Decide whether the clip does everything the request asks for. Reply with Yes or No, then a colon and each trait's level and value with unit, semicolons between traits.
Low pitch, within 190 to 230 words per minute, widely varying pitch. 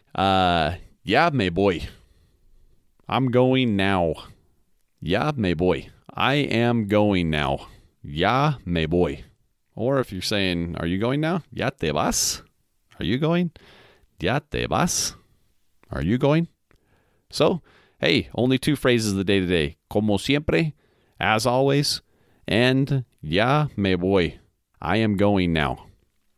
No: low, 105 Hz; slow, 135 wpm; wide, 6.4 semitones